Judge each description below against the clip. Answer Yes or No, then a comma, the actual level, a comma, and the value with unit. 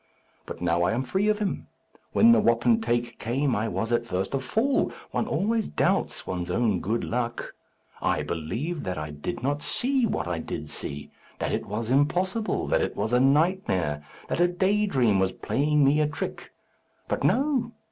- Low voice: Yes, low, 130 Hz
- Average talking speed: Yes, average, 185 wpm